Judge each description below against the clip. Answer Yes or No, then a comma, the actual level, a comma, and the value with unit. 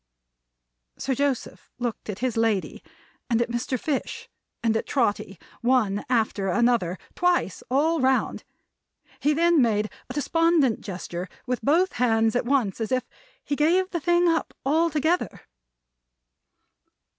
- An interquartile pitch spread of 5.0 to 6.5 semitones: Yes, wide, 5.6 semitones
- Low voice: No, very high, 255 Hz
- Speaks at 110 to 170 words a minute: Yes, slow, 135 wpm